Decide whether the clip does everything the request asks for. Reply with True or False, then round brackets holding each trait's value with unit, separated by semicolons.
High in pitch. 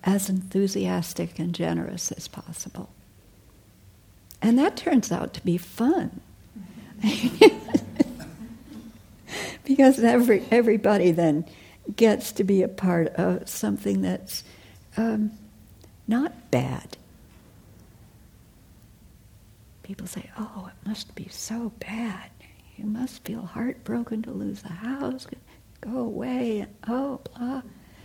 True (195 Hz)